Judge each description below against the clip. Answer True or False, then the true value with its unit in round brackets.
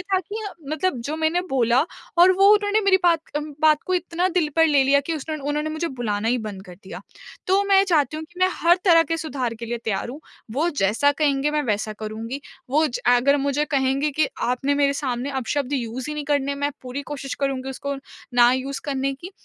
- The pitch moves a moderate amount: True (3.7 semitones)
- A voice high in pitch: True (285 Hz)